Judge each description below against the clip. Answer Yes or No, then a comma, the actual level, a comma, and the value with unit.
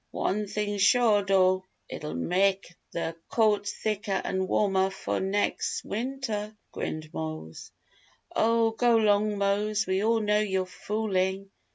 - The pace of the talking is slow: Yes, slow, 130 wpm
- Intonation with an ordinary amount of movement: No, narrow, 2.1 semitones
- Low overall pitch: No, high, 205 Hz